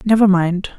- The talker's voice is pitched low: No, high, 190 Hz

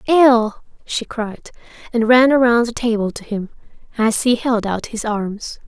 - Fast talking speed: No, average, 170 wpm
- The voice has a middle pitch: No, high, 230 Hz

